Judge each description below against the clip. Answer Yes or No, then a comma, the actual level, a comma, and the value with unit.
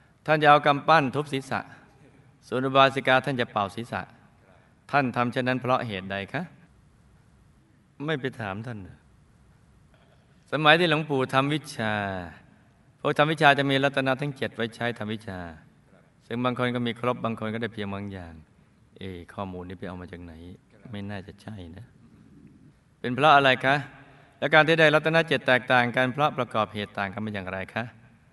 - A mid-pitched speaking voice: No, low, 125 Hz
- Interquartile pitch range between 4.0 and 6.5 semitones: Yes, average, 5.2 semitones